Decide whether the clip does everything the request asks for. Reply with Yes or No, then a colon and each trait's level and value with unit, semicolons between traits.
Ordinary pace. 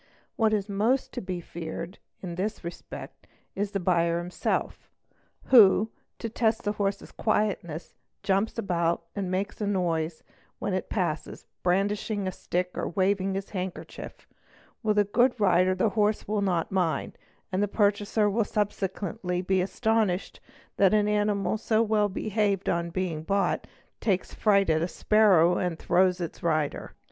Yes: average, 155 wpm